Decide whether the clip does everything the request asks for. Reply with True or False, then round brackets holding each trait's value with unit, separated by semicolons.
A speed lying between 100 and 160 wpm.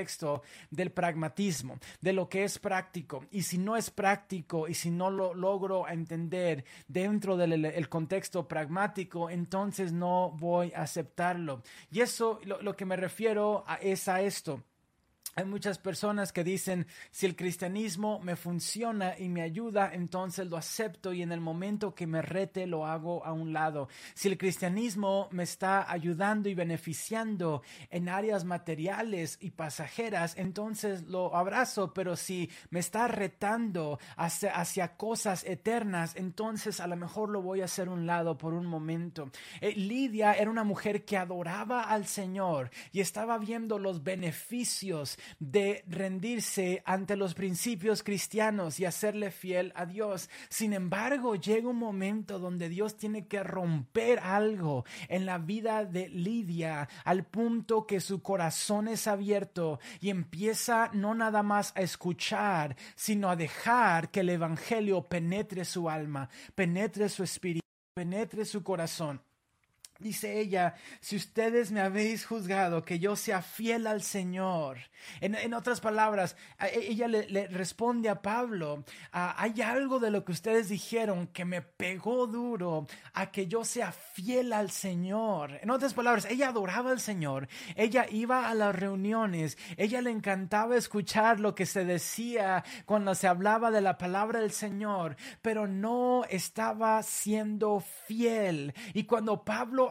True (155 wpm)